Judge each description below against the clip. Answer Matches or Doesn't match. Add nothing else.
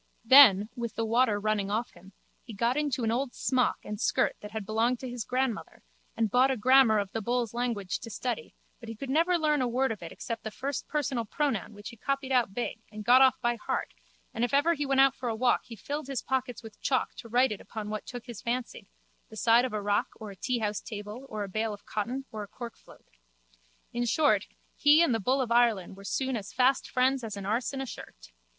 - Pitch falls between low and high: Doesn't match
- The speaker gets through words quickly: Matches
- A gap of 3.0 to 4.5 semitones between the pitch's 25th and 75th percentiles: Matches